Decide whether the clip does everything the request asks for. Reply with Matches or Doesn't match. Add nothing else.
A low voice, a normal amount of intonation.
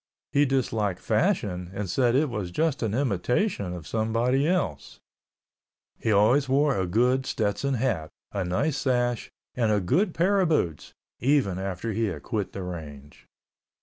Doesn't match